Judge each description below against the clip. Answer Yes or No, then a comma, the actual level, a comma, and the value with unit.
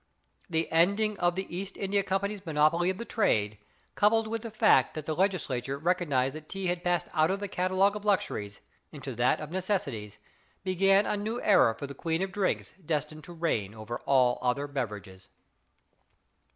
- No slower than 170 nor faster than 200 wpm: Yes, average, 180 wpm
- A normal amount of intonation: No, wide, 6.1 semitones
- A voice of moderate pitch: Yes, medium, 175 Hz